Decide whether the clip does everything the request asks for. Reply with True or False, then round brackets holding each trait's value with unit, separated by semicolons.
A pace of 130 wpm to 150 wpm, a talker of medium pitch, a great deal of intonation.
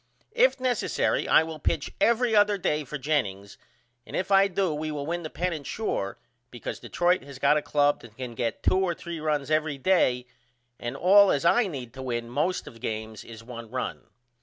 False (205 wpm; 150 Hz; 6.6 semitones)